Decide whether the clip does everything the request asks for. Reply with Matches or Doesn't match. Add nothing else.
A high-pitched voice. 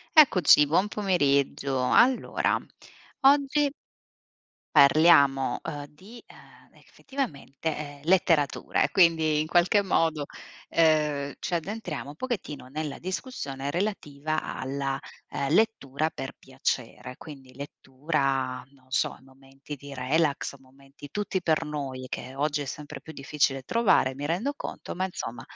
Doesn't match